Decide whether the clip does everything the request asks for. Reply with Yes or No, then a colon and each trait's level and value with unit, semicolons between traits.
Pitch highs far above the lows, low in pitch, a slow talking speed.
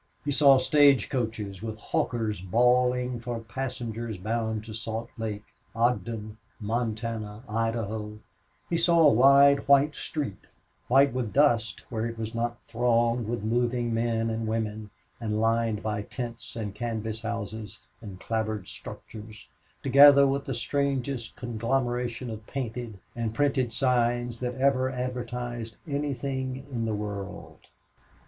No: narrow, 2.4 semitones; low, 115 Hz; slow, 130 wpm